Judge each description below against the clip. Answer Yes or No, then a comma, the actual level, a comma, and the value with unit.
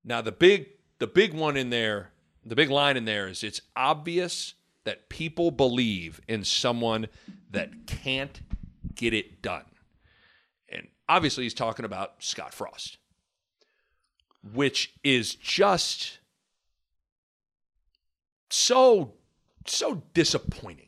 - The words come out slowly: Yes, slow, 110 wpm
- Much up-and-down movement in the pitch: Yes, wide, 7.7 semitones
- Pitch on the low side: Yes, low, 115 Hz